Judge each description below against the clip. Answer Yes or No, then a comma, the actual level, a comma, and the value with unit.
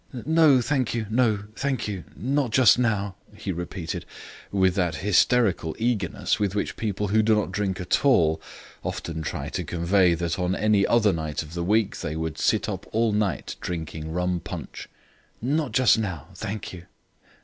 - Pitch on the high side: No, low, 100 Hz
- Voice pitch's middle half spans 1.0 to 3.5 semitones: No, average, 4.4 semitones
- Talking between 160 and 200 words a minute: Yes, average, 170 wpm